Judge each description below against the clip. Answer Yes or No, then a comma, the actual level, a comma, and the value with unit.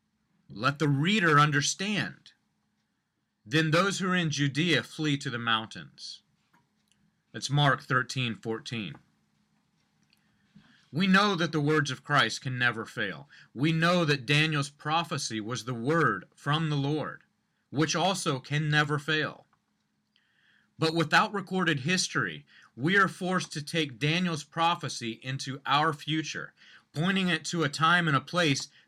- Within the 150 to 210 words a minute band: No, slow, 135 wpm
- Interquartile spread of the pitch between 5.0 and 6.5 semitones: No, average, 3.7 semitones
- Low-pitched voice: No, medium, 150 Hz